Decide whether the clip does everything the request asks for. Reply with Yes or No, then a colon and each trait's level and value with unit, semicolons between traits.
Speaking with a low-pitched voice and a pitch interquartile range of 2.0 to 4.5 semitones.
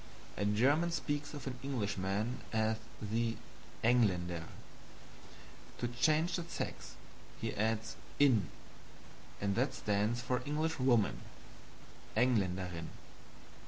No: low, 115 Hz; average, 5.0 semitones